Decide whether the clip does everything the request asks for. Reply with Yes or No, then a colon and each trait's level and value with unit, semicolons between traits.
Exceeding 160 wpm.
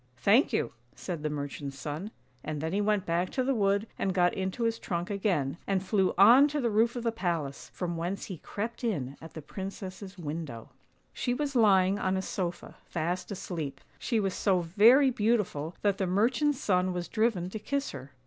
Yes: average, 200 wpm